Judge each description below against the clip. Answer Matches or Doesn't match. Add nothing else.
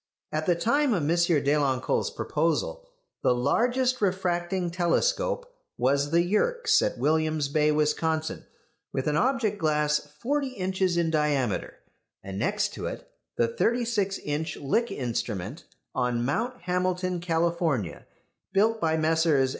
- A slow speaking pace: Matches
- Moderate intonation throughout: Doesn't match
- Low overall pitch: Doesn't match